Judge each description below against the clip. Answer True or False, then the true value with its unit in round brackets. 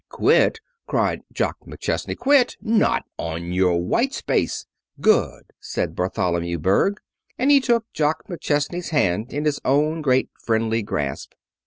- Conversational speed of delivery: False (130 wpm)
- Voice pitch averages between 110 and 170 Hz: True (140 Hz)